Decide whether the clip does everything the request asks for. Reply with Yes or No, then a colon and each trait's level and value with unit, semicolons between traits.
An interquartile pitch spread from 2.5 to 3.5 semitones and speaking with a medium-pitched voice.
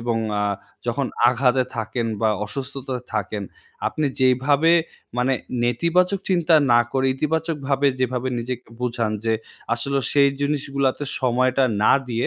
No: average, 2.8 semitones; low, 130 Hz